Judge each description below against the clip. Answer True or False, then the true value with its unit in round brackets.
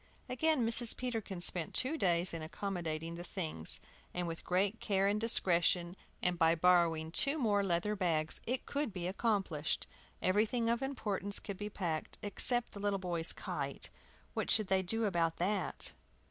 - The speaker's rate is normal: True (160 wpm)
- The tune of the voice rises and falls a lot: False (4.3 semitones)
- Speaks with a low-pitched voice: False (190 Hz)